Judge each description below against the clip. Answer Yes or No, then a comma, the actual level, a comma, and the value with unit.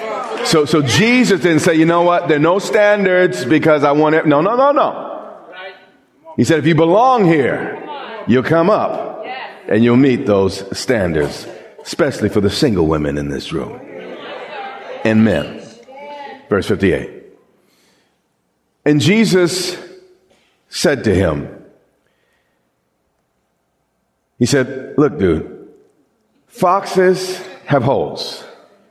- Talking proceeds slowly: Yes, slow, 120 wpm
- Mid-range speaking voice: Yes, medium, 165 Hz